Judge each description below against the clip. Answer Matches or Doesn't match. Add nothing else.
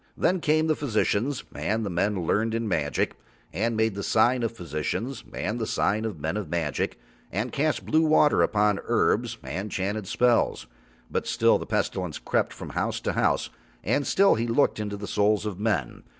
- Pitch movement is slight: Doesn't match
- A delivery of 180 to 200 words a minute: Matches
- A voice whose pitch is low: Matches